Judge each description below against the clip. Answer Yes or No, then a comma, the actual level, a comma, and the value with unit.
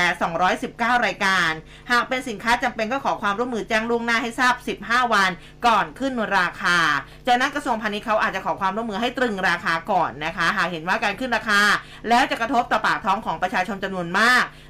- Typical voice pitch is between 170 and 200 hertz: No, high, 225 Hz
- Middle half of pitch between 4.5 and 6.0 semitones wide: No, average, 3.7 semitones